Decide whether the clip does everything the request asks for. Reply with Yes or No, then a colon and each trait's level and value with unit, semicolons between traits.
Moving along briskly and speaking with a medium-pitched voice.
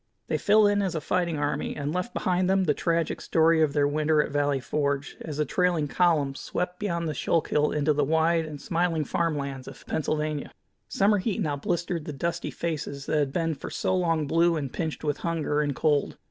Yes: fast, 210 wpm; medium, 155 Hz